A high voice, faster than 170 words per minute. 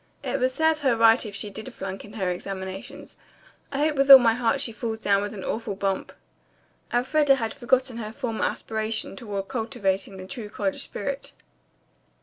Yes: high, 225 Hz; average, 180 wpm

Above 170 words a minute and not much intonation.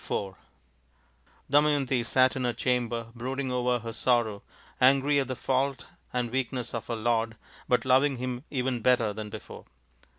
No: average, 155 wpm; narrow, 2.1 semitones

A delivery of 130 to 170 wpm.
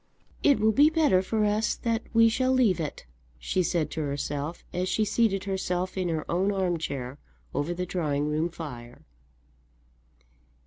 Yes: average, 165 wpm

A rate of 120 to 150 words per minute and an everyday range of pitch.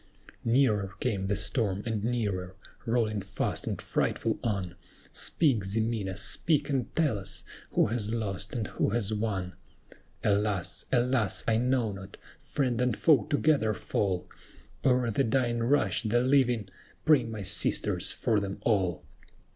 Yes: average, 140 wpm; average, 3.8 semitones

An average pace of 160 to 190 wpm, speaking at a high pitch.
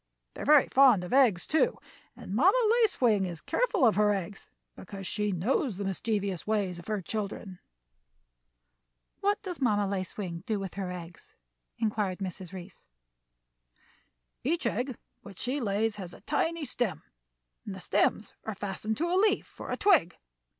Yes: average, 165 wpm; high, 210 Hz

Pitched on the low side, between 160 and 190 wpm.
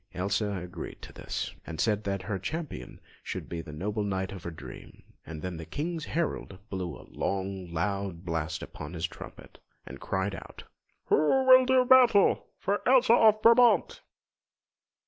Yes: low, 100 Hz; average, 165 wpm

